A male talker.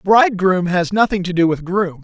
Yes: male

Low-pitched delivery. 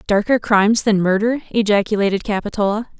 No: high, 210 Hz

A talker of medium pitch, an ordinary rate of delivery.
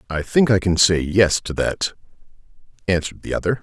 No: very low, 95 Hz; average, 180 wpm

